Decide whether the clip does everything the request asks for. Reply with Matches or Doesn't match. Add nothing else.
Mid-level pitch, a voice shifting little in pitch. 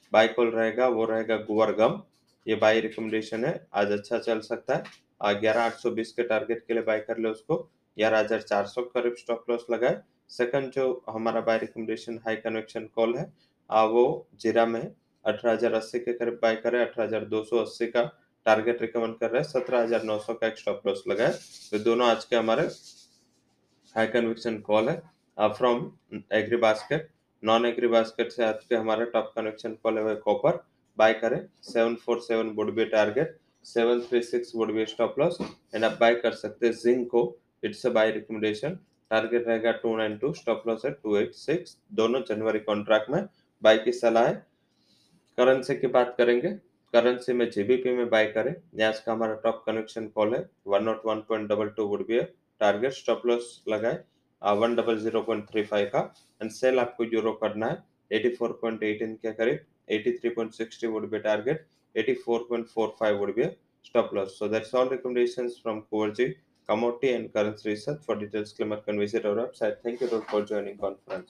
Doesn't match